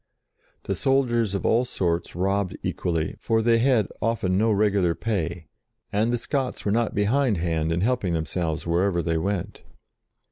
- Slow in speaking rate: No, average, 155 wpm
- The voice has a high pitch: No, low, 100 Hz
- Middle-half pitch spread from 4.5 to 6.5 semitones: Yes, average, 4.9 semitones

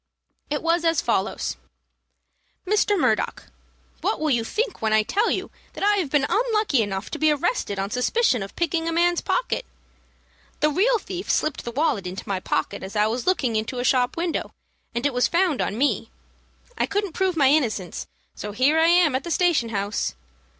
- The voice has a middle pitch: No, very high, 295 Hz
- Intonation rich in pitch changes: Yes, wide, 7.6 semitones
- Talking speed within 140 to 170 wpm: No, average, 190 wpm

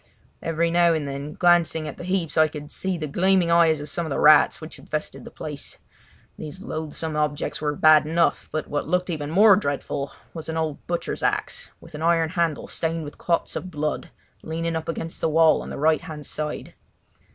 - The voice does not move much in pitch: Yes, narrow, 1.9 semitones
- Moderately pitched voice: Yes, medium, 160 Hz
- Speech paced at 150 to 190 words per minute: No, fast, 205 wpm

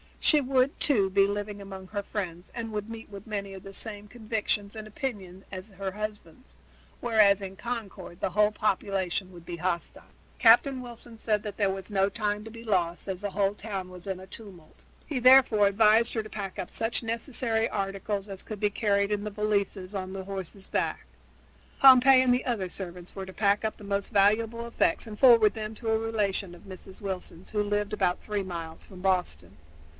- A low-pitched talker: No, high, 205 Hz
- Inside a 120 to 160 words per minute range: No, average, 200 wpm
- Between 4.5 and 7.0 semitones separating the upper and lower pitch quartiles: No, narrow, 2.5 semitones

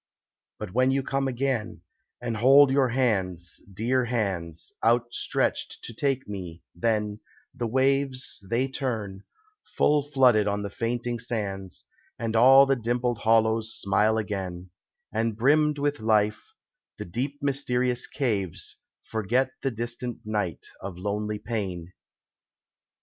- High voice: No, low, 115 Hz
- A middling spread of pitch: Yes, average, 4.0 semitones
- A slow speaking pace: Yes, slow, 125 wpm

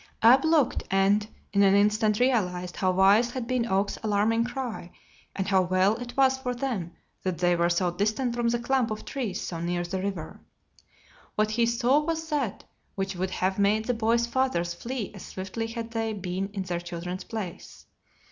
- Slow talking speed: No, average, 185 wpm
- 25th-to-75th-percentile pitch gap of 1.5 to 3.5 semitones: No, average, 4.3 semitones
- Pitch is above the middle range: Yes, high, 210 Hz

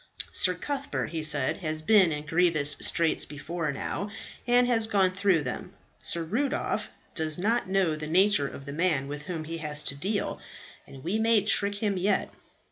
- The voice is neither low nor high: Yes, medium, 175 Hz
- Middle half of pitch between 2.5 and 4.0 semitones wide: No, average, 4.9 semitones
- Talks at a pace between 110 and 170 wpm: No, average, 180 wpm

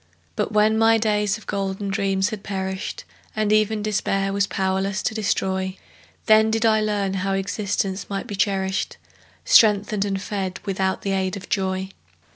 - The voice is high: Yes, high, 195 Hz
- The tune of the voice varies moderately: No, narrow, 1.7 semitones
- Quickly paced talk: No, average, 160 wpm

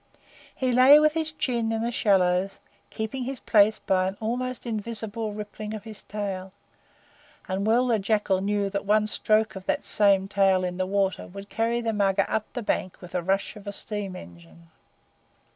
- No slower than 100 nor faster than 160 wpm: No, average, 185 wpm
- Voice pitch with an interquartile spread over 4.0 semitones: No, average, 2.8 semitones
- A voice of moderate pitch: No, high, 210 Hz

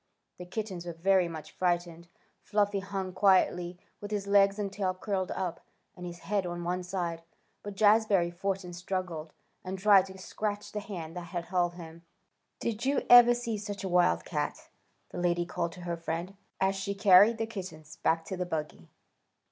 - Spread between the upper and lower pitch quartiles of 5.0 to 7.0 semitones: No, average, 2.7 semitones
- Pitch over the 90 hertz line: Yes, medium, 185 Hz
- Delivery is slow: No, average, 180 wpm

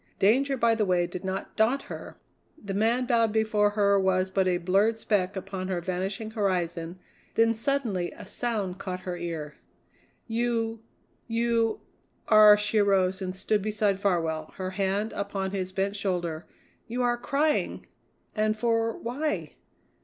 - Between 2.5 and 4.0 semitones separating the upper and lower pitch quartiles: Yes, average, 3.4 semitones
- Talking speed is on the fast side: No, average, 150 wpm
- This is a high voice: Yes, high, 200 Hz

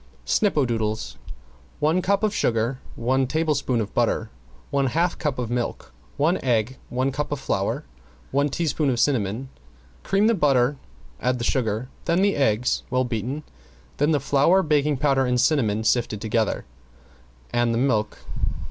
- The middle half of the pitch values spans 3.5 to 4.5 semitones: Yes, average, 4.1 semitones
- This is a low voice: Yes, low, 130 Hz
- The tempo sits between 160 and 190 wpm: No, average, 150 wpm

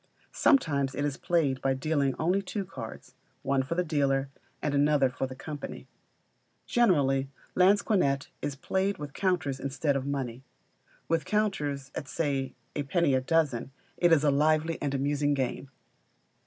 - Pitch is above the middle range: No, medium, 145 Hz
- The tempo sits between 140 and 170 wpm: Yes, average, 155 wpm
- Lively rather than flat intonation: No, average, 3.4 semitones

